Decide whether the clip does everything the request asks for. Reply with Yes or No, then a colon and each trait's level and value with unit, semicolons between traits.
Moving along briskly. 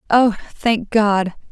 No: slow, 120 wpm